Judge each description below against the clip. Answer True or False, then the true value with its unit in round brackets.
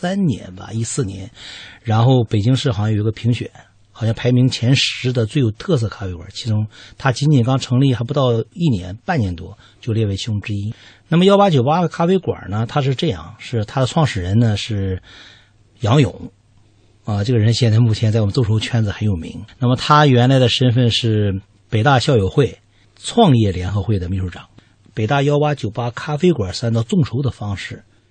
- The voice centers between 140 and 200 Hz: False (115 Hz)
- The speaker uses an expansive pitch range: False (4.3 semitones)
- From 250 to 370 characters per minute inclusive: True (290 characters per minute)